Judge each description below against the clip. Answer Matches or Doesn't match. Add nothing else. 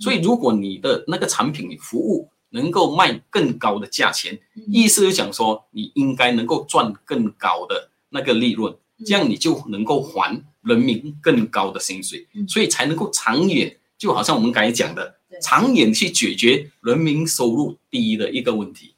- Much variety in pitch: Matches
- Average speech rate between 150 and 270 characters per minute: Matches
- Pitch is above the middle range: Matches